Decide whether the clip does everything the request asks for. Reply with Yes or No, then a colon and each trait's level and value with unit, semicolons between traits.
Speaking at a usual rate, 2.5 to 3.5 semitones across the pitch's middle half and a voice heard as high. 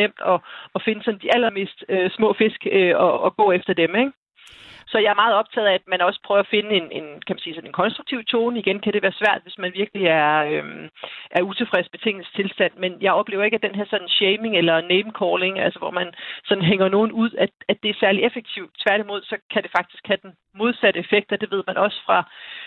No: fast, 240 wpm; average, 2.9 semitones; high, 200 Hz